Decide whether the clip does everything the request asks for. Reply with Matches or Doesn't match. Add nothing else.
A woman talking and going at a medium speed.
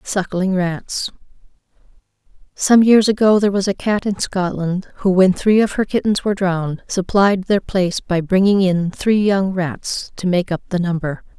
Matches